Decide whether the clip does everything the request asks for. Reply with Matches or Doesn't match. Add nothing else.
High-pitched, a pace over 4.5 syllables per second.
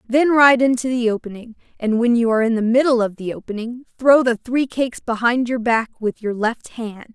Matches